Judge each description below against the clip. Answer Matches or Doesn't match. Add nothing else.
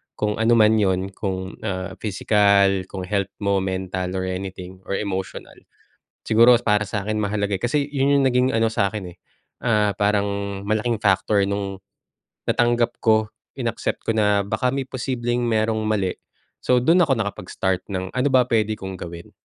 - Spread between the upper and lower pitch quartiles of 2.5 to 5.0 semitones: Matches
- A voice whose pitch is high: Doesn't match